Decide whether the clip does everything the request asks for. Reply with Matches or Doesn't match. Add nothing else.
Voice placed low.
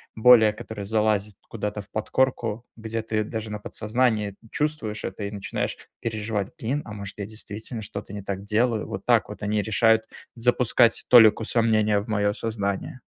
Matches